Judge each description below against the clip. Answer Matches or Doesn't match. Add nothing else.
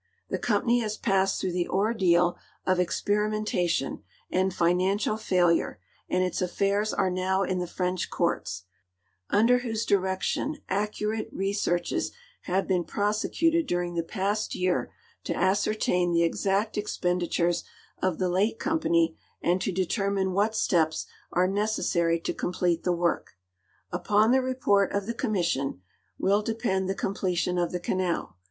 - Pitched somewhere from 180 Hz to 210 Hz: Matches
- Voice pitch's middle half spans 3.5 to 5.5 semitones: Doesn't match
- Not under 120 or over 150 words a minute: Matches